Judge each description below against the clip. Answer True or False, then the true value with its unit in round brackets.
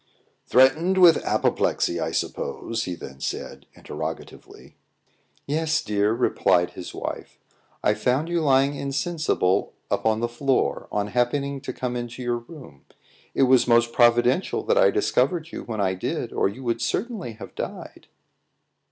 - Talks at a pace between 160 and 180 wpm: False (145 wpm)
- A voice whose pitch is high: False (125 Hz)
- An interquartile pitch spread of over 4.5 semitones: True (4.9 semitones)